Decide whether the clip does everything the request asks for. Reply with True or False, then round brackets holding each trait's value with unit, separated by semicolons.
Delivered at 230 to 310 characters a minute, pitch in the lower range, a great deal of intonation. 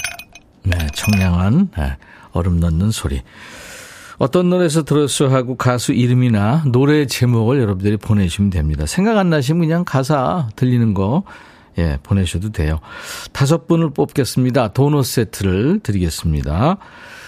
True (300 characters per minute; 125 Hz; 7.6 semitones)